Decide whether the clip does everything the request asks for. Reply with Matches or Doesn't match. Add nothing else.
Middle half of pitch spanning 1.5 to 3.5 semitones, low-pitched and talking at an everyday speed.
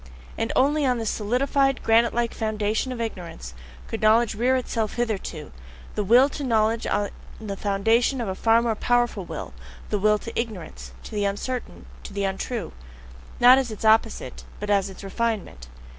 Doesn't match